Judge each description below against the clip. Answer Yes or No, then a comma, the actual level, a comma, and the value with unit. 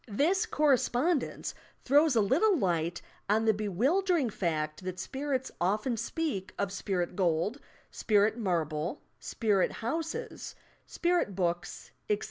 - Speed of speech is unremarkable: No, slow, 115 wpm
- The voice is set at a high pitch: Yes, high, 215 Hz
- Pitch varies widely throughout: Yes, wide, 8.0 semitones